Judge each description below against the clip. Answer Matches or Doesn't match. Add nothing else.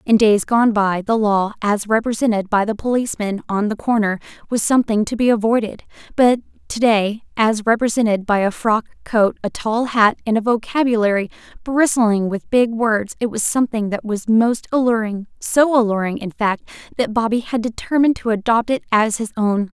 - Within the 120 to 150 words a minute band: Doesn't match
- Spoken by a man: Doesn't match